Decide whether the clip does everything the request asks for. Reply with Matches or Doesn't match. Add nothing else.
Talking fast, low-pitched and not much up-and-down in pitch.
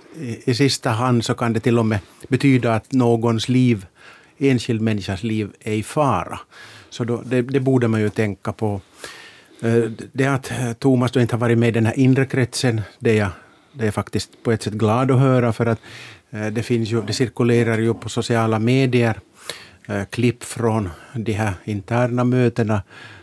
Doesn't match